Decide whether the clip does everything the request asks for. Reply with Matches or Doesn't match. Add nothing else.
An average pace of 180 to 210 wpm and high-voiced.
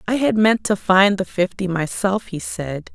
Matches